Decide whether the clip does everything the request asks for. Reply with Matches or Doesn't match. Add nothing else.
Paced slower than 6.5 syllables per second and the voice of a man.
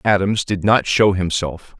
Matches